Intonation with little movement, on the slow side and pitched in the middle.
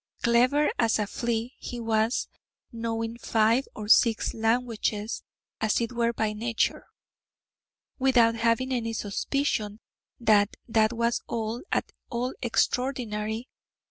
No: narrow, 1.7 semitones; slow, 110 wpm; high, 230 Hz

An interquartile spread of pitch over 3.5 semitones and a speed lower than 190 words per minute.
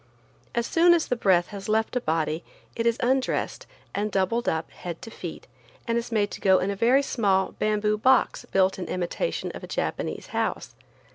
No: average, 3.9 semitones; average, 195 wpm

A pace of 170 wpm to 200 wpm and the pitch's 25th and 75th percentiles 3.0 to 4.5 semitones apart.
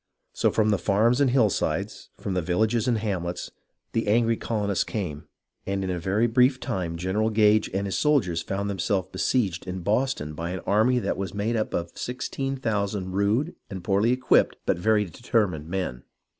Yes: average, 175 wpm; average, 3.7 semitones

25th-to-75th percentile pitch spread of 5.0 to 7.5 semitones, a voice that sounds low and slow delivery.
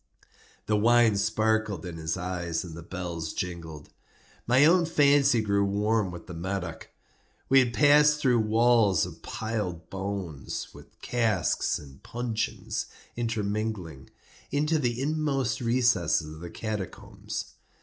Yes: wide, 5.5 semitones; low, 110 Hz; slow, 130 wpm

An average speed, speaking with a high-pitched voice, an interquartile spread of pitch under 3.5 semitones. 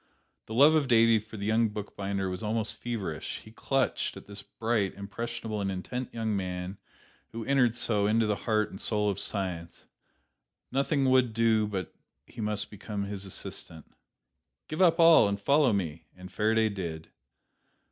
No: average, 165 wpm; low, 110 Hz; average, 2.8 semitones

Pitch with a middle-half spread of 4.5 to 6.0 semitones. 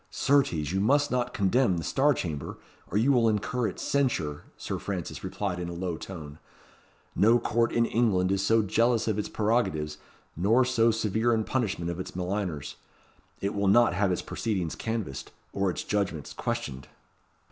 Yes: average, 4.8 semitones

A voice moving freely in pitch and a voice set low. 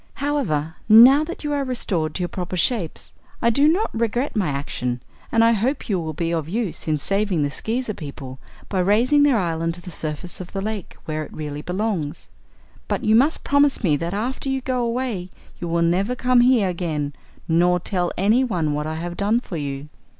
No: wide, 6.9 semitones; high, 190 Hz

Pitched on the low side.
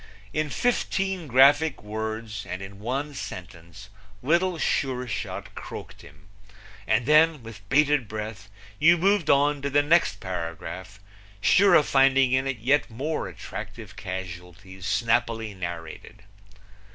Yes: low, 120 Hz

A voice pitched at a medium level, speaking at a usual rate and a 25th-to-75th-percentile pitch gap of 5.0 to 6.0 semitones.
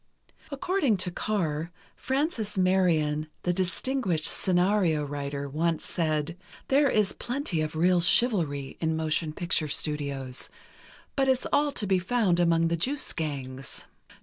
No: medium, 175 Hz; slow, 130 wpm; wide, 5.6 semitones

